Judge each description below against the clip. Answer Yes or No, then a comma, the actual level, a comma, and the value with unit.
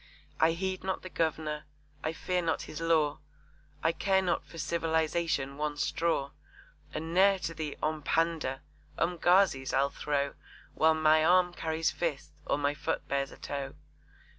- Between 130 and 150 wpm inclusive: Yes, average, 145 wpm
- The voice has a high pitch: No, medium, 160 Hz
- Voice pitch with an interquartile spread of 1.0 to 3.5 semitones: Yes, narrow, 2.5 semitones